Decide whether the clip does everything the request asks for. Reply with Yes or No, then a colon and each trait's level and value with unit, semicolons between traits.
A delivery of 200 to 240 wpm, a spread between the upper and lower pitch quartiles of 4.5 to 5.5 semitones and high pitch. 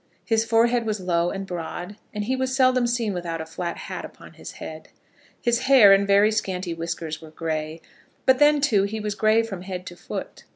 Yes: fast, 205 wpm; average, 5.0 semitones; high, 200 Hz